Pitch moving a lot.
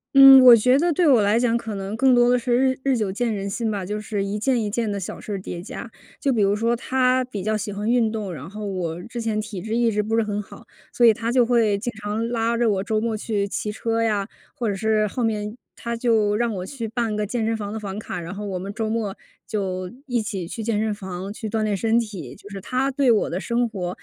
No: narrow, 2.6 semitones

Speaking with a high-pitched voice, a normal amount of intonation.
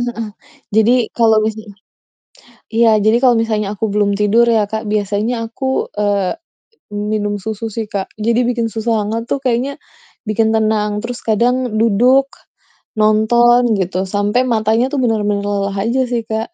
No: high, 220 Hz; narrow, 2.2 semitones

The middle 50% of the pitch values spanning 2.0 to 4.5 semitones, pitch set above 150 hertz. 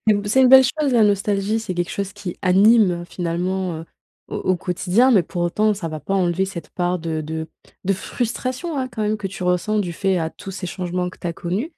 Yes: average, 3.5 semitones; high, 190 Hz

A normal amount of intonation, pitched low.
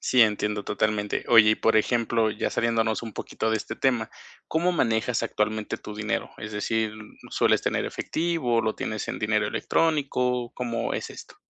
No: narrow, 2.2 semitones; low, 110 Hz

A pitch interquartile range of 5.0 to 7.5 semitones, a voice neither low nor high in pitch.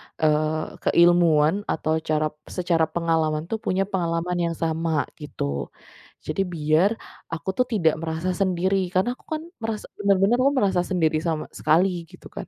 No: average, 3.2 semitones; medium, 170 Hz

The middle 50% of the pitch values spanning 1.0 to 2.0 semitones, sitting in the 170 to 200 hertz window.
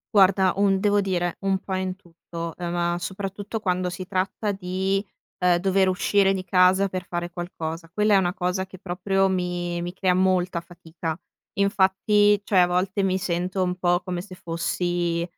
Yes: narrow, 1.7 semitones; medium, 185 Hz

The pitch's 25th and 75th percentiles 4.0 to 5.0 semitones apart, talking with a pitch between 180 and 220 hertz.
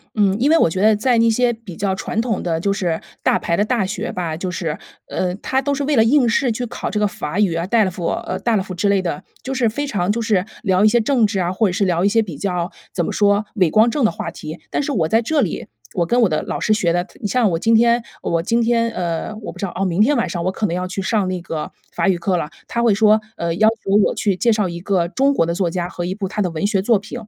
Yes: average, 4.3 semitones; high, 200 Hz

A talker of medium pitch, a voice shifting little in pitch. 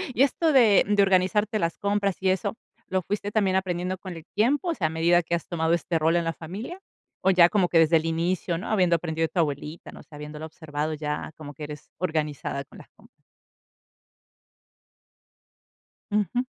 No: medium, 175 Hz; average, 3.8 semitones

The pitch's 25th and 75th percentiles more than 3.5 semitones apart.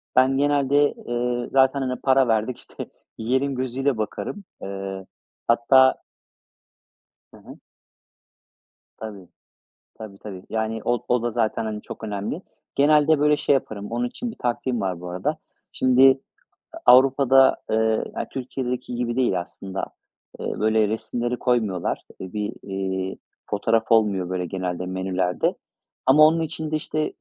Yes: average, 4.7 semitones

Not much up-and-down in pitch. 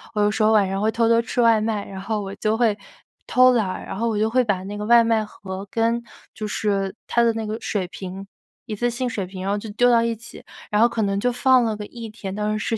Yes: narrow, 2.3 semitones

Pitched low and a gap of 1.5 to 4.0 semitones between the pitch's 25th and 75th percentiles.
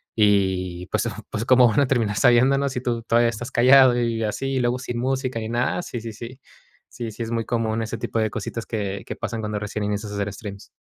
Yes: low, 115 Hz; narrow, 2.6 semitones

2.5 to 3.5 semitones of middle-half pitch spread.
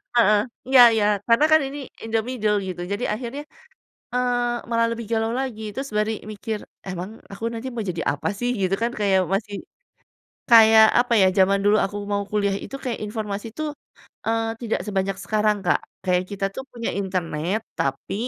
Yes: average, 2.9 semitones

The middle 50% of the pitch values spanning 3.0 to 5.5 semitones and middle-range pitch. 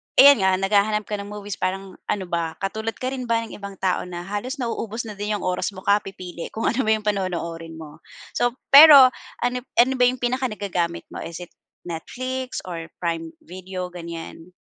No: average, 4.5 semitones; high, 200 Hz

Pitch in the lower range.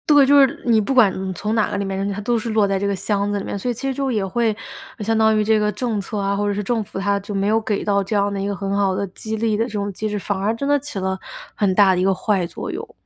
No: high, 205 Hz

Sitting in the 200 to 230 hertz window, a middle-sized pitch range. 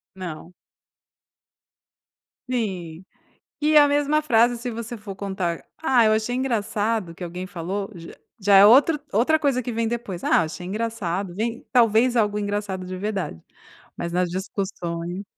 Yes: high, 205 Hz; average, 4.5 semitones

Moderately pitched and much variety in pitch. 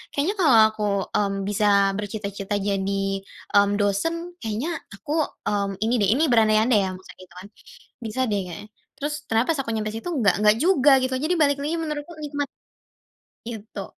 No: high, 220 Hz; wide, 6.1 semitones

